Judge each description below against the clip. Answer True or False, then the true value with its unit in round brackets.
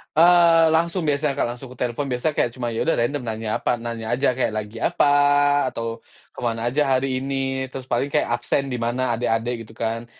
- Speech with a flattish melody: False (3.4 semitones)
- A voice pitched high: False (130 Hz)